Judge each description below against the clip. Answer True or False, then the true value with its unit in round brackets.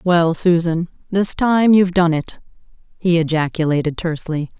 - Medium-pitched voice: True (170 Hz)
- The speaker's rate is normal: False (130 wpm)